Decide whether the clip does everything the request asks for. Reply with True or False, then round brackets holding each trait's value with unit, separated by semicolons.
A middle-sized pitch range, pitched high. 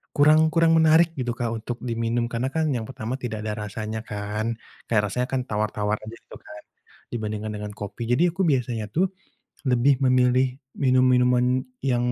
False (3.1 semitones; 120 Hz)